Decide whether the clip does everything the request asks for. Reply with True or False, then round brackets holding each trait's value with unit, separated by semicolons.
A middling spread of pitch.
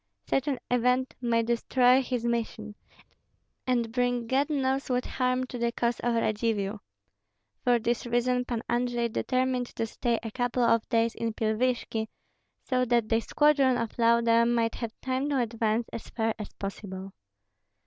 False (1.7 semitones)